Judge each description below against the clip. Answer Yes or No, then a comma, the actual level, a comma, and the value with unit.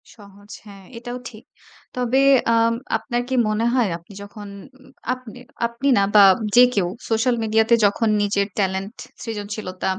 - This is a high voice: Yes, high, 220 Hz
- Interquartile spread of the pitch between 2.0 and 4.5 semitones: Yes, average, 2.9 semitones